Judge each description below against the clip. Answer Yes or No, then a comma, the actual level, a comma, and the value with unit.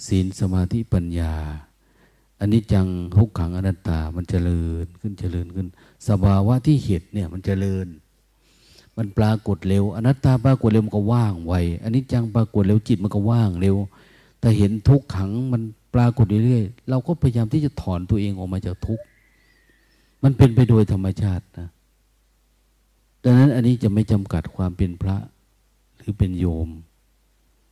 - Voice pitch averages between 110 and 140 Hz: No, low, 100 Hz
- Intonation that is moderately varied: Yes, average, 3.9 semitones